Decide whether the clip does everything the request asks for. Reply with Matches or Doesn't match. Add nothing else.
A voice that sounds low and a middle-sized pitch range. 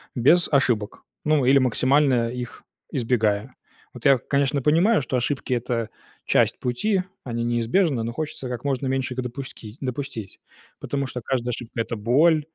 Matches